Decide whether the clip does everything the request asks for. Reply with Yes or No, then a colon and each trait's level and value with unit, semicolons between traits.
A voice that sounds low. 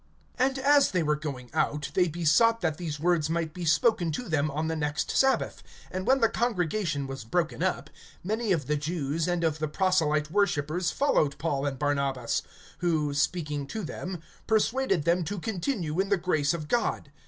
No: medium, 165 Hz